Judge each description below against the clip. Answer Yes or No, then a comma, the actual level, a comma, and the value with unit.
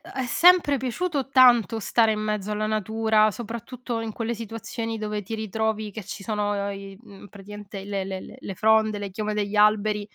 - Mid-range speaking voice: No, high, 215 Hz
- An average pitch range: No, narrow, 1.7 semitones